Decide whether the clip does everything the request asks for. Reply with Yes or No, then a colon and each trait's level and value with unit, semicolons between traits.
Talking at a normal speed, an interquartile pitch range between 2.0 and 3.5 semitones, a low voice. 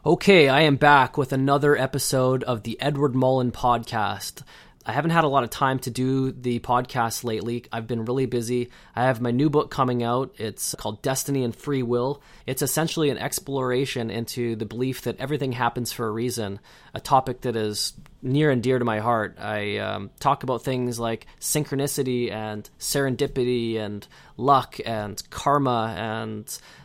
Yes: average, 175 wpm; average, 3.1 semitones; low, 125 Hz